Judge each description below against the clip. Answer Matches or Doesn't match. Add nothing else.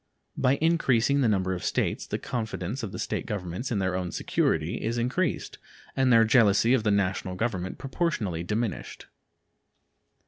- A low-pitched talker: Matches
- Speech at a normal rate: Matches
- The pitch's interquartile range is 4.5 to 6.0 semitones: Matches